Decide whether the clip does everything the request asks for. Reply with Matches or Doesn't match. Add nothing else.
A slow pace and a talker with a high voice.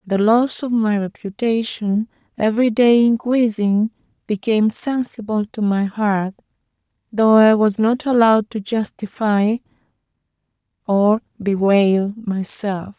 Matches